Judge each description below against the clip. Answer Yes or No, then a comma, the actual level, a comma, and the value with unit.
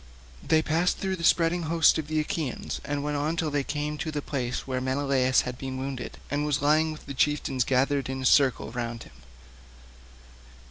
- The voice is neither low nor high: Yes, medium, 145 Hz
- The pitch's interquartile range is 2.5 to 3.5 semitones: Yes, average, 2.9 semitones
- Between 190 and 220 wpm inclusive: Yes, average, 195 wpm